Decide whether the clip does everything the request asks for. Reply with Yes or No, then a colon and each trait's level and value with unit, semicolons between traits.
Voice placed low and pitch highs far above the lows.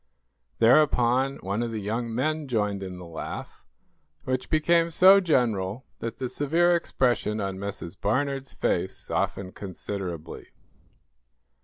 Yes: low, 120 Hz; wide, 5.9 semitones